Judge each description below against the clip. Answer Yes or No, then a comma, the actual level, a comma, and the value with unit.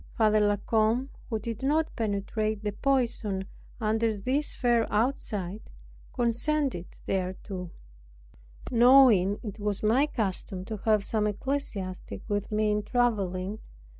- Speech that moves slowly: Yes, slow, 120 wpm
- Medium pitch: No, high, 215 Hz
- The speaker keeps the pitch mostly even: No, average, 3.1 semitones